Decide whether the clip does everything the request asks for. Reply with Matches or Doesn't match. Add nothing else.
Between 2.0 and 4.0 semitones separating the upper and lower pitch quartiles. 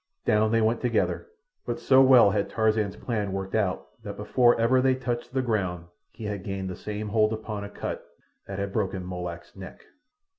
Matches